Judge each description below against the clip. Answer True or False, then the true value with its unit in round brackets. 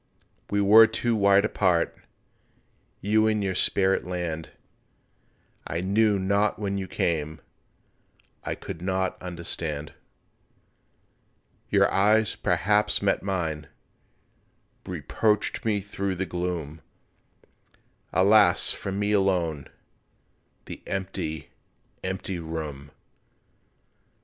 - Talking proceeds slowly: True (95 wpm)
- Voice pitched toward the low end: True (95 Hz)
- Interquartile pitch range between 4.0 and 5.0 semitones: False (3.3 semitones)